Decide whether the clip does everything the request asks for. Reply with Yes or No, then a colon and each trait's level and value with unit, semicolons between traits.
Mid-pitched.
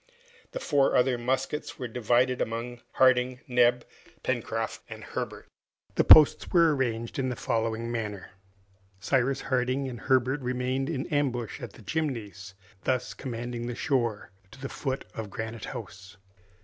No: low, 125 Hz